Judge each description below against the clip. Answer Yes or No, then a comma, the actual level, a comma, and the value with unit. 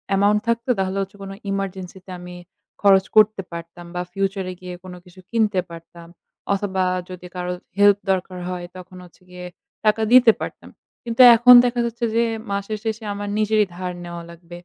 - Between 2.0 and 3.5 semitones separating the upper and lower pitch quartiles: Yes, average, 2.9 semitones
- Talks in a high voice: Yes, high, 195 Hz